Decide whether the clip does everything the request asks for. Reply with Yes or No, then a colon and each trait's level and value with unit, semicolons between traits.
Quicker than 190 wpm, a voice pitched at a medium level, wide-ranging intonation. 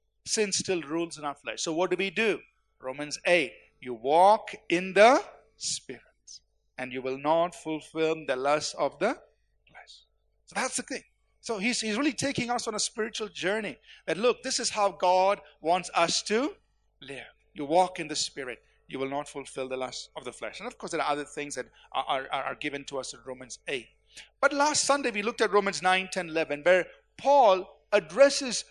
Yes: average, 200 wpm; medium, 180 Hz; wide, 6.8 semitones